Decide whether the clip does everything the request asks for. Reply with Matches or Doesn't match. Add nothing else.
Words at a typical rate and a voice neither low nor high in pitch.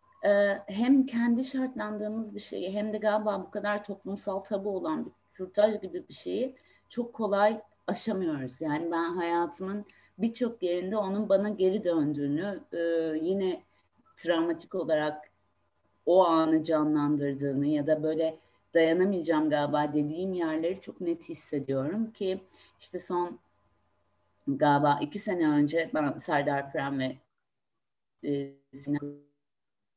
Matches